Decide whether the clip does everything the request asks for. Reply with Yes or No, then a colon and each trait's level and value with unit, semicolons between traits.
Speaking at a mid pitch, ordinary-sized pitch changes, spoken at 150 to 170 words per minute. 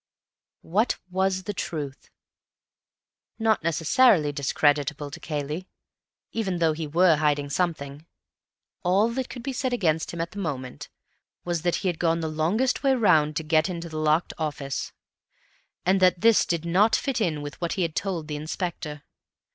Yes: medium, 170 Hz; average, 3.9 semitones; average, 165 wpm